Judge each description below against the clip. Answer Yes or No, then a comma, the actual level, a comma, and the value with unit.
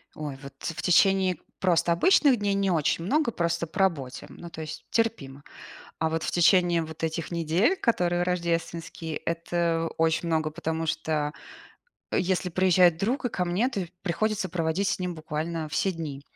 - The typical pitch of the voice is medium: Yes, medium, 170 Hz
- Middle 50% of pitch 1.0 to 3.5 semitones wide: Yes, average, 2.7 semitones